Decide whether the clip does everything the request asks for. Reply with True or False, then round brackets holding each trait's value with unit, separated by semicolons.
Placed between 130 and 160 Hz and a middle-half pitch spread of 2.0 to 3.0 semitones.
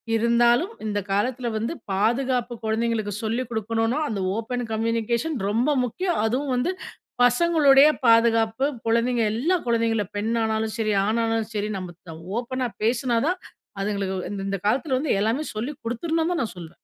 False (230 Hz; 2.7 semitones)